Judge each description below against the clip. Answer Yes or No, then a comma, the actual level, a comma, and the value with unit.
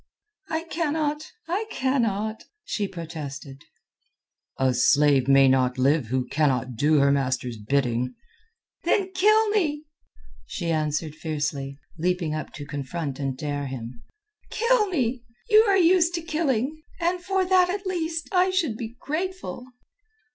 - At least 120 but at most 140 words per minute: Yes, slow, 135 wpm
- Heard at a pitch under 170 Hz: No, medium, 180 Hz